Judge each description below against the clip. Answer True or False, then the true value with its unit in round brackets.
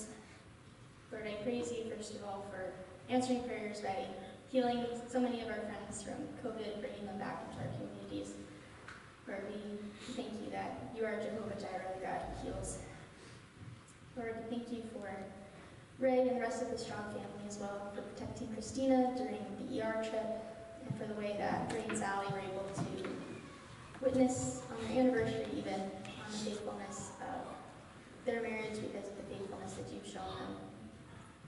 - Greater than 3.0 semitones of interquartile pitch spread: True (3.5 semitones)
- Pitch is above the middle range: True (220 Hz)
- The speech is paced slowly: False (175 wpm)